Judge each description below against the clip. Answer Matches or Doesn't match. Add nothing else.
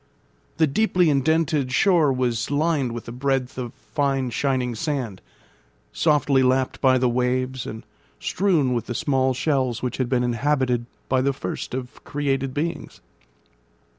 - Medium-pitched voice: Doesn't match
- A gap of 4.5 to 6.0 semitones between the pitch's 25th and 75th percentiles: Doesn't match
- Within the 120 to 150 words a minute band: Matches